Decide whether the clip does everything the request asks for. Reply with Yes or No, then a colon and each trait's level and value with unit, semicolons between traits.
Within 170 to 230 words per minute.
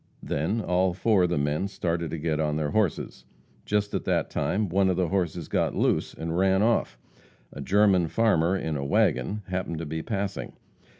Yes: average, 190 wpm